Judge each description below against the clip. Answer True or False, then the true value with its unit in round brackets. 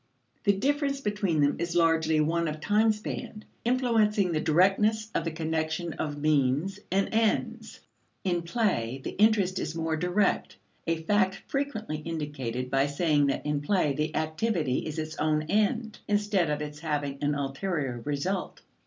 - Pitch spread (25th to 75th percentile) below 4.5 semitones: False (5.5 semitones)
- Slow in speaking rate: False (155 wpm)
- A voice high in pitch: False (165 Hz)